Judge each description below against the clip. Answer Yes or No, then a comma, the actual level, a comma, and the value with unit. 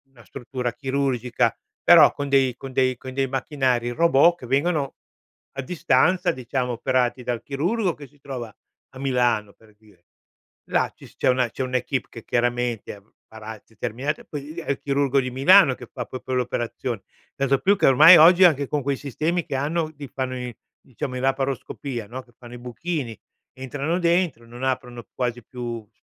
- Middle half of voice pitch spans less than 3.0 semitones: Yes, narrow, 2.6 semitones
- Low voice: Yes, low, 130 Hz